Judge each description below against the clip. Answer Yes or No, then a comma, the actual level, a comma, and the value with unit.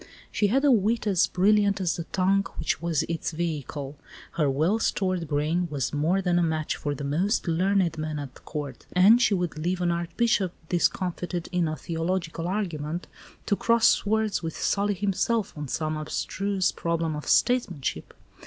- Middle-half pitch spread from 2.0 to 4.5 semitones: Yes, average, 4.1 semitones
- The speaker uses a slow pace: No, average, 170 wpm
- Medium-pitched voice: Yes, medium, 175 Hz